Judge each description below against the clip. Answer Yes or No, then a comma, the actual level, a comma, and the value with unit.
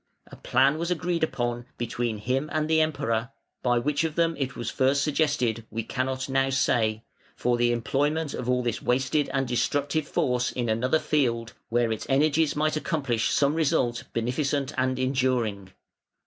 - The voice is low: Yes, low, 130 Hz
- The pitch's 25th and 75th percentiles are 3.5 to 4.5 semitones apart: Yes, average, 3.8 semitones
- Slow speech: No, average, 165 wpm